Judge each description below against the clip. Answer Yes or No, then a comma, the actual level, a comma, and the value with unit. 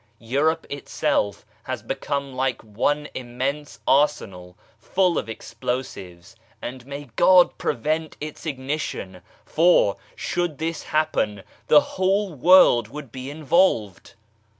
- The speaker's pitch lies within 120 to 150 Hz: Yes, medium, 140 Hz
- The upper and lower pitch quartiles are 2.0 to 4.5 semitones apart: No, average, 5.1 semitones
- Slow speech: Yes, slow, 110 wpm